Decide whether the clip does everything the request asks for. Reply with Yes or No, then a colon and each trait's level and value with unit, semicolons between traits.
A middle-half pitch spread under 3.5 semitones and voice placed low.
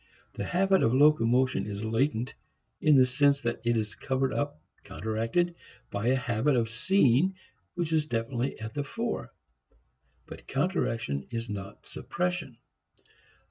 No: average, 4.7 semitones; low, 125 Hz